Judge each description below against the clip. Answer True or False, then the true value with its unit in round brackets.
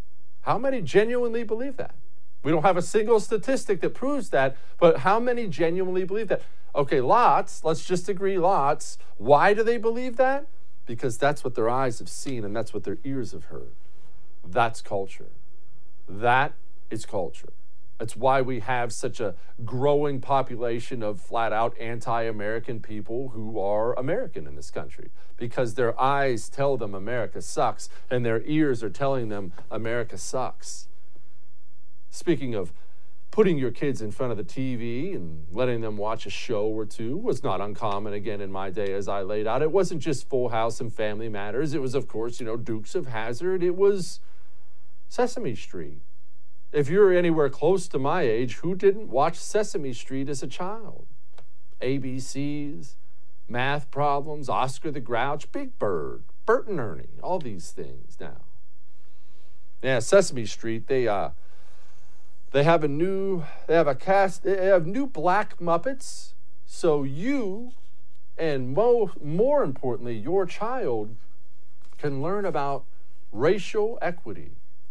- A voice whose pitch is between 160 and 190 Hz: False (135 Hz)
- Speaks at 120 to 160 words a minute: True (150 wpm)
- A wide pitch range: True (7.9 semitones)